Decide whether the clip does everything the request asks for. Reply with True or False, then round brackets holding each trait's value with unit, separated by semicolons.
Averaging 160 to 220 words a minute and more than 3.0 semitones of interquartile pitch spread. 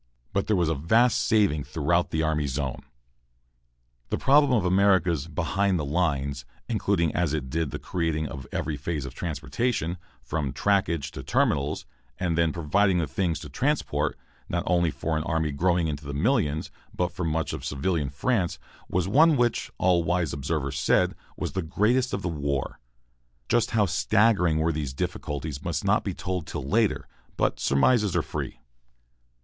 True (170 wpm; 4.5 semitones)